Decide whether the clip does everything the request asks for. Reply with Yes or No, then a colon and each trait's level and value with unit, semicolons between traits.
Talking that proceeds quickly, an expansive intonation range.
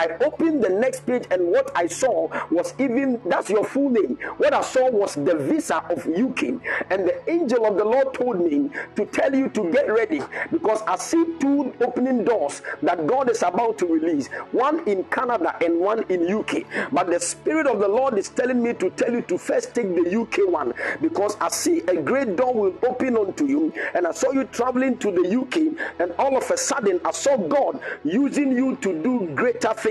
Yes: fast, 215 wpm; wide, 6.0 semitones